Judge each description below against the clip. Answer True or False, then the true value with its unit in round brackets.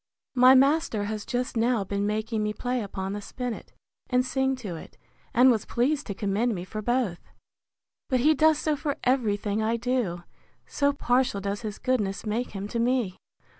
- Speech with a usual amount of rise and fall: True (3.9 semitones)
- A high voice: True (235 Hz)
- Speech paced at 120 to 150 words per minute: False (185 wpm)